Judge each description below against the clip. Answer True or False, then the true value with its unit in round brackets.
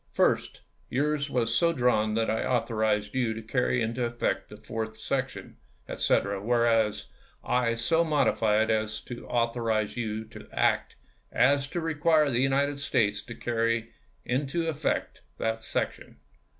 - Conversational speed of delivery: True (150 wpm)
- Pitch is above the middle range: False (120 Hz)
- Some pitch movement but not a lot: True (3.6 semitones)